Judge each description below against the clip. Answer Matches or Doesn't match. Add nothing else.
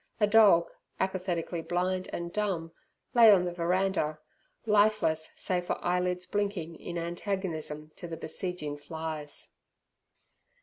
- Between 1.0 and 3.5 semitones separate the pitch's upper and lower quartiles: Matches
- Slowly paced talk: Matches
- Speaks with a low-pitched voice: Doesn't match